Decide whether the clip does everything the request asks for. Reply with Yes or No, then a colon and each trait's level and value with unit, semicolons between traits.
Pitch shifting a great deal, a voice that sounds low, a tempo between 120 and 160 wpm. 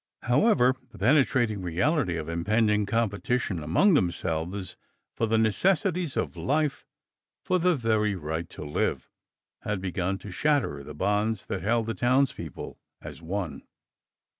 Yes: wide, 6.3 semitones; low, 105 Hz; slow, 135 wpm